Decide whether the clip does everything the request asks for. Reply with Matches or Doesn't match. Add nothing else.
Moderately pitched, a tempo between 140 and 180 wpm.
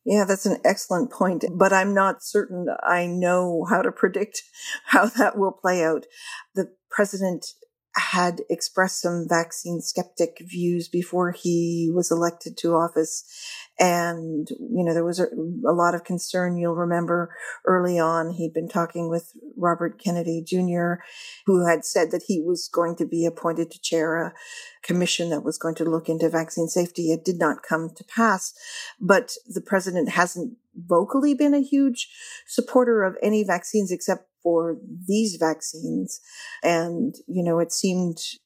Matches